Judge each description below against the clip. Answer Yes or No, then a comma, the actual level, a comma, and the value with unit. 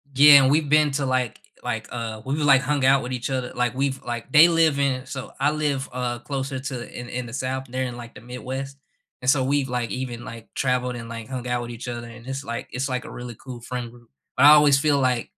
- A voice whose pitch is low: Yes, low, 130 Hz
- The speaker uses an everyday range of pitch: No, narrow, 2.2 semitones